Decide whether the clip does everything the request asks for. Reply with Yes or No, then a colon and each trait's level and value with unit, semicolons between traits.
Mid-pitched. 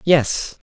Yes: medium, 145 Hz